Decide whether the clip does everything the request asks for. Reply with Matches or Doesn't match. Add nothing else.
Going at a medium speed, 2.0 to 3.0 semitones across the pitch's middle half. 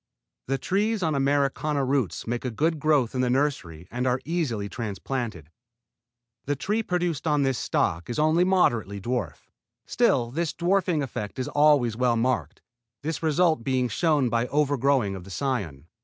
Doesn't match